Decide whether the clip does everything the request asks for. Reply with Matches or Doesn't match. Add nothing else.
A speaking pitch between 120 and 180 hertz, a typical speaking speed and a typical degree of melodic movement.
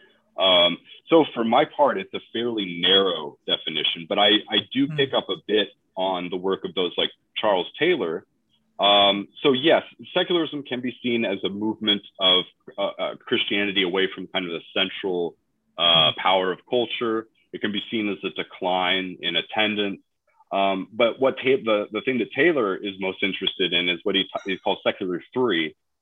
Doesn't match